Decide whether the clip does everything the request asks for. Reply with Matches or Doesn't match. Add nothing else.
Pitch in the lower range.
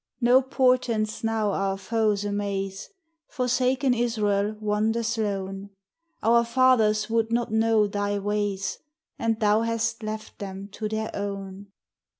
Doesn't match